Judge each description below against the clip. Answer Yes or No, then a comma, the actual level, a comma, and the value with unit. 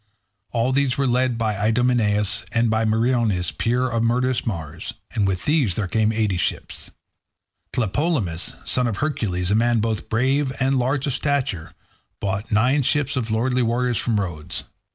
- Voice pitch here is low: Yes, low, 115 Hz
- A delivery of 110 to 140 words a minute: No, average, 160 wpm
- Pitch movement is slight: No, average, 3.5 semitones